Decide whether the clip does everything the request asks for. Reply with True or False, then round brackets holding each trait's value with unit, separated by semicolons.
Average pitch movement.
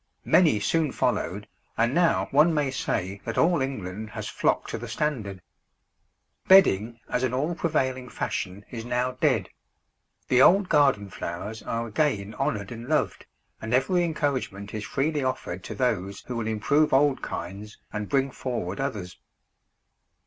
False (5.7 semitones)